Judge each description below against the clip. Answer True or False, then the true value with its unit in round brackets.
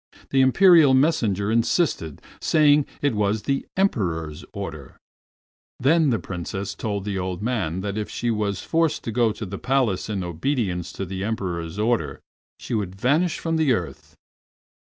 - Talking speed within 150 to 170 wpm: True (160 wpm)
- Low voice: True (105 Hz)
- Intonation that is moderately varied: False (6.4 semitones)